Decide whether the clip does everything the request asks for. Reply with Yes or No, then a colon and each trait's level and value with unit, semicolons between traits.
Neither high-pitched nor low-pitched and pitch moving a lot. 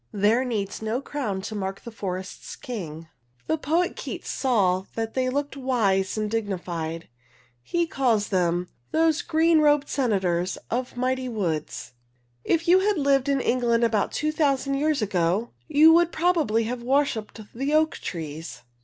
No: high, 240 Hz; wide, 6.8 semitones